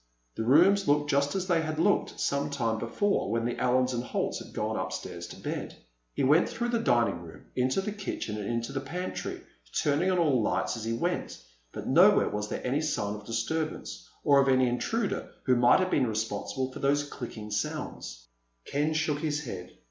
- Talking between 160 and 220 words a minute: Yes, average, 200 wpm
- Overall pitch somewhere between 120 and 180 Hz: Yes, low, 135 Hz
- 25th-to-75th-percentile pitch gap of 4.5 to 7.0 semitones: Yes, average, 5.3 semitones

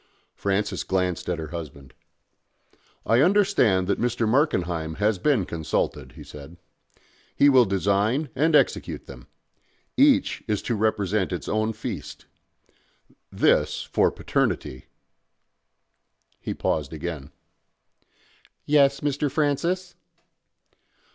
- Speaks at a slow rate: Yes, slow, 110 wpm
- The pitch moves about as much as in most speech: No, wide, 8.2 semitones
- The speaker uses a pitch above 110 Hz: No, low, 105 Hz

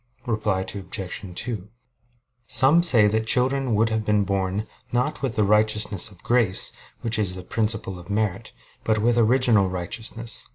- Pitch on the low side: Yes, low, 110 Hz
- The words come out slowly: No, average, 155 wpm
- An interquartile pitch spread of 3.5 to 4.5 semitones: No, average, 2.9 semitones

